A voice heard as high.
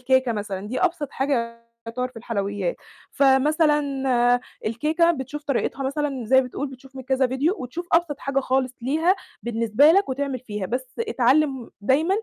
Yes: very high, 265 Hz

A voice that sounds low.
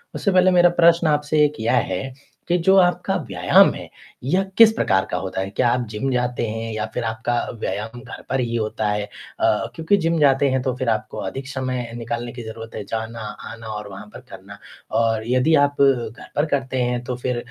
Yes: low, 125 Hz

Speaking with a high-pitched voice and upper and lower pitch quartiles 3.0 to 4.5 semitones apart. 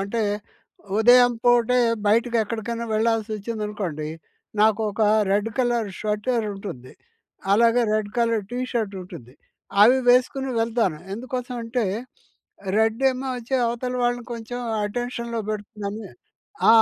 No: high, 230 Hz; narrow, 2.5 semitones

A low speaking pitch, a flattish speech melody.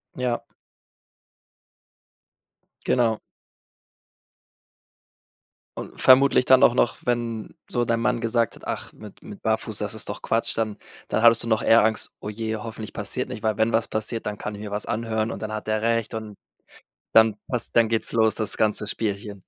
Yes: low, 110 Hz; narrow, 1.4 semitones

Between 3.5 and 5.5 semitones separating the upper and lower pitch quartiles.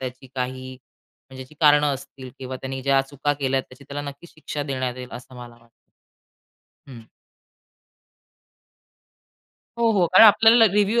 No: narrow, 2.5 semitones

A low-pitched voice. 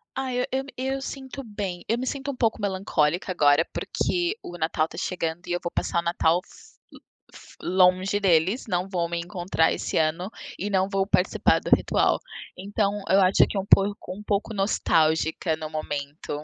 No: medium, 185 Hz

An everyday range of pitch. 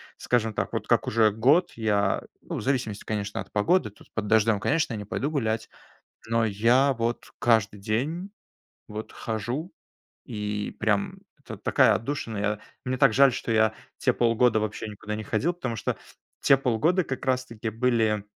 Yes: average, 3.3 semitones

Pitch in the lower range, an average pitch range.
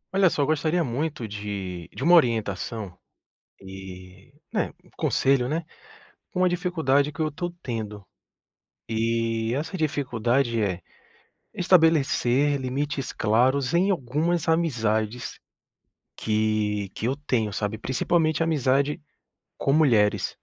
No: low, 130 Hz; wide, 6.2 semitones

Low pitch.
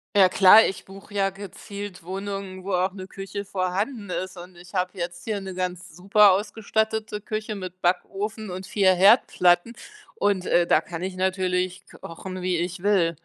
No: high, 190 Hz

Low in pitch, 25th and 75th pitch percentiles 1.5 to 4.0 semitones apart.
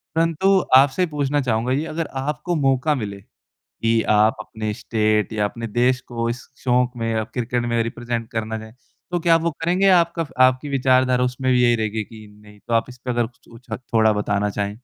Yes: low, 120 Hz; average, 3.5 semitones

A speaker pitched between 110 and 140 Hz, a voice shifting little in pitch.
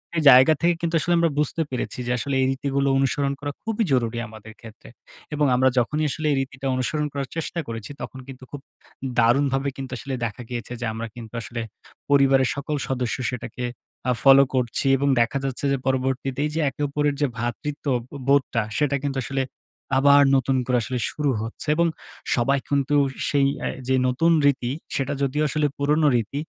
Yes: low, 135 Hz; narrow, 2.3 semitones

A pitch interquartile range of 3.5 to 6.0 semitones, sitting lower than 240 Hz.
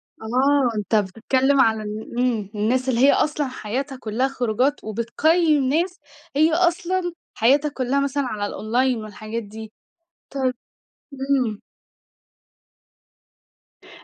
No: average, 4.3 semitones; very high, 255 Hz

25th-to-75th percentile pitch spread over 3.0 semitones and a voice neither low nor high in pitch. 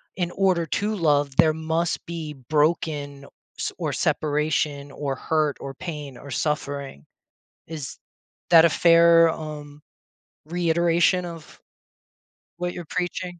No: average, 2.7 semitones; medium, 160 Hz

